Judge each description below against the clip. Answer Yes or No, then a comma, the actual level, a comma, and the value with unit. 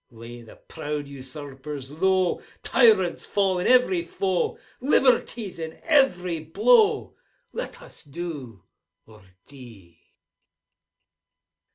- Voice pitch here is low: No, medium, 165 Hz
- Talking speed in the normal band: No, slow, 100 wpm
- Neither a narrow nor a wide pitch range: No, wide, 6.7 semitones